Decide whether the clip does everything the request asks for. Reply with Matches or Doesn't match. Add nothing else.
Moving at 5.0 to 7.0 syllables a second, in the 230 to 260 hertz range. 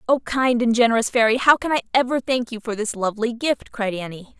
Matches